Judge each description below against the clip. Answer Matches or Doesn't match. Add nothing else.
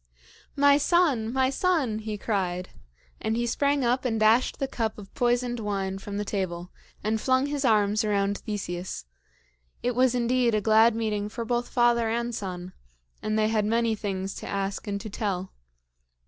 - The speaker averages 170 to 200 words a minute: Matches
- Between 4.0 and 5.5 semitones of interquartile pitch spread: Doesn't match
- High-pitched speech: Matches